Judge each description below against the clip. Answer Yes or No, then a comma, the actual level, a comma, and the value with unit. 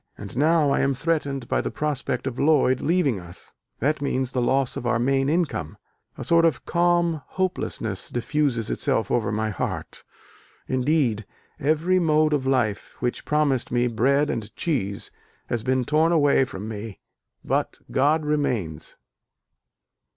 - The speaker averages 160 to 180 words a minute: No, average, 150 wpm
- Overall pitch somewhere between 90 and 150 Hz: Yes, low, 135 Hz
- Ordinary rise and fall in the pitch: Yes, average, 4.5 semitones